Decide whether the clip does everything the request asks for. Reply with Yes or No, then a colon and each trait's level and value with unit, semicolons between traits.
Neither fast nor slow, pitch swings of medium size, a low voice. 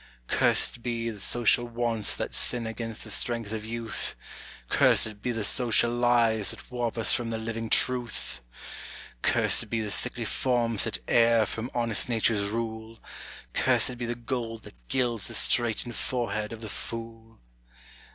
No: average, 155 wpm; narrow, 1.3 semitones; low, 115 Hz